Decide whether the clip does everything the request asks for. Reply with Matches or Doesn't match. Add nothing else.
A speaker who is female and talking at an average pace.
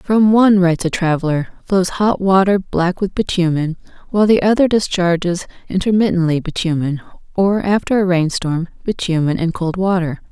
Matches